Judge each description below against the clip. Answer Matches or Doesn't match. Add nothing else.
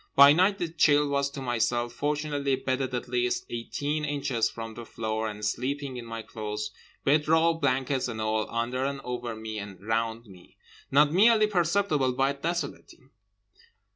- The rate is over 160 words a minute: Doesn't match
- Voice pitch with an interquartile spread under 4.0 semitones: Doesn't match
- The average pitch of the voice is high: Doesn't match